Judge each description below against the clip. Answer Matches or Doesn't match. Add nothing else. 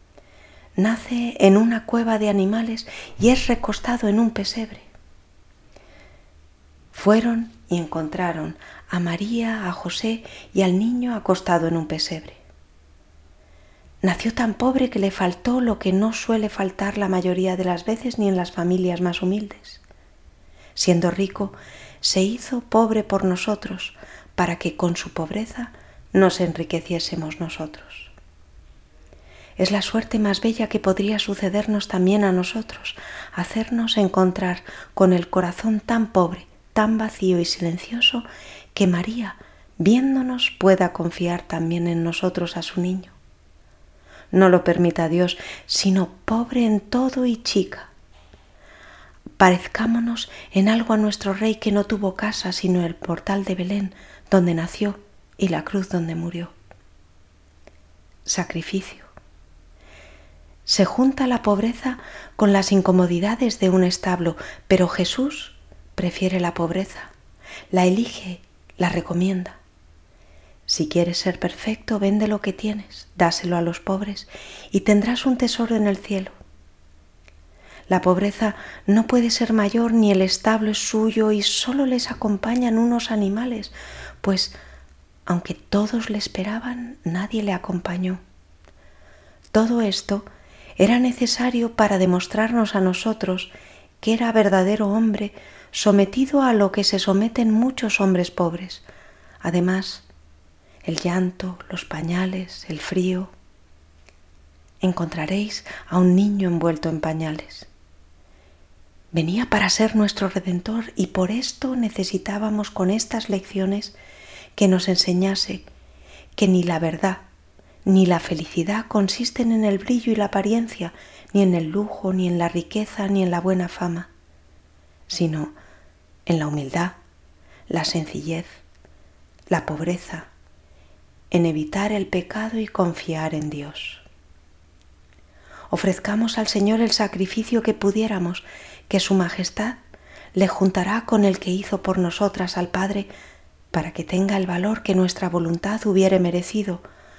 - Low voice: Doesn't match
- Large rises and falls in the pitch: Doesn't match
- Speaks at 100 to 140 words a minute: Matches